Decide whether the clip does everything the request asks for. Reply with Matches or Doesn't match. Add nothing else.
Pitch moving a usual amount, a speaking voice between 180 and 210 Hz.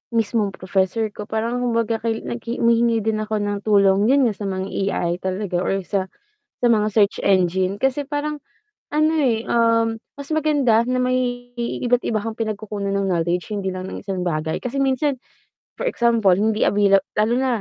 Doesn't match